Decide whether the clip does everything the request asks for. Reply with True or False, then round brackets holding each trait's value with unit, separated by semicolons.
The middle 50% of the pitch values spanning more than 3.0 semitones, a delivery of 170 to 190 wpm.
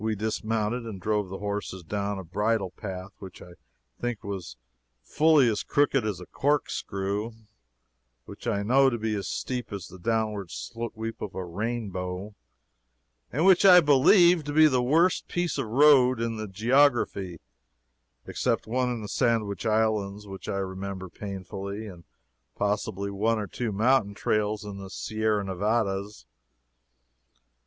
False (3.5 semitones; 150 wpm)